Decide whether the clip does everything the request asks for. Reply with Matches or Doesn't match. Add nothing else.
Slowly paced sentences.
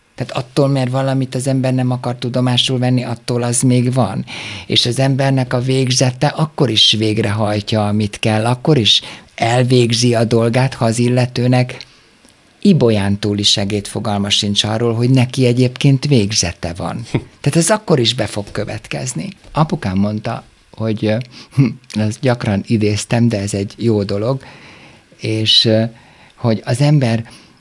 Doesn't match